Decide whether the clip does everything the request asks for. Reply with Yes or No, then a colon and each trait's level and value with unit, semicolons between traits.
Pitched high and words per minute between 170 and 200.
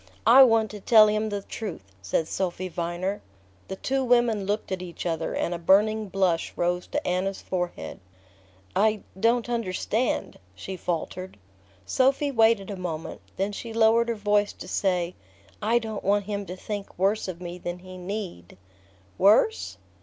No: high, 200 Hz; average, 160 wpm